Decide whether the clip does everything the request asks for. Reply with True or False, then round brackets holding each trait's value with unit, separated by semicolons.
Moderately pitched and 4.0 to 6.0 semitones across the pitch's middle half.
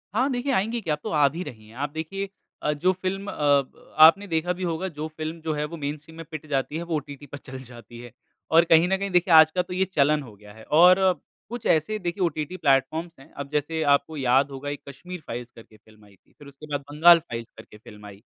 True (155 Hz; 4.3 semitones)